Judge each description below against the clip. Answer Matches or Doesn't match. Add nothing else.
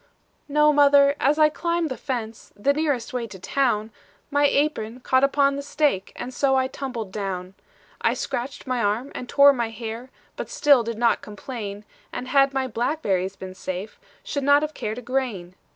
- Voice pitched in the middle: Doesn't match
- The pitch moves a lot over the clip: Doesn't match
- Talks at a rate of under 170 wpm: Doesn't match